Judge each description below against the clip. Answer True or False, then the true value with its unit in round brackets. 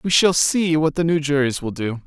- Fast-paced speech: True (260 wpm)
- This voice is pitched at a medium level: True (150 Hz)